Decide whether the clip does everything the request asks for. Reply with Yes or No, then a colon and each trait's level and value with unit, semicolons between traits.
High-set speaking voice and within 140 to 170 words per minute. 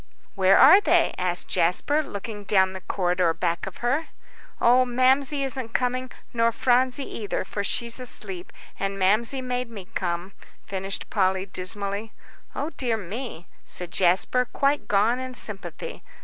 Yes: high, 220 Hz; average, 145 wpm